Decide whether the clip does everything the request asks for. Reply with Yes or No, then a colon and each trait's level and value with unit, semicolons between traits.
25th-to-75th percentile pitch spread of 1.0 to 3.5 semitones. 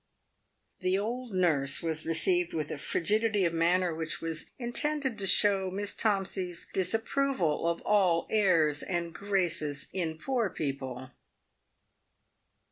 No: average, 4.1 semitones